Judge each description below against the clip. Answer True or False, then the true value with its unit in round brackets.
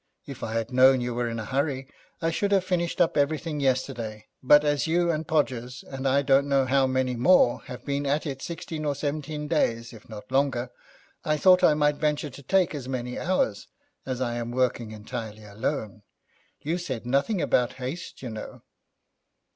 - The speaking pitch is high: False (135 Hz)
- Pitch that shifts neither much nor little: True (3.6 semitones)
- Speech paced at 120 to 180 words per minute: False (190 wpm)